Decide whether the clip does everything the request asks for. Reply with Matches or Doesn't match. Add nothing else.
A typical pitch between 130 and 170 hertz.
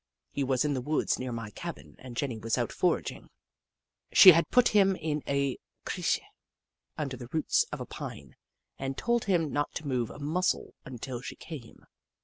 Matches